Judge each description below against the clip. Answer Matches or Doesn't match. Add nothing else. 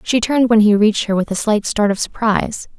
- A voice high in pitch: Matches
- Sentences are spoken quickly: Matches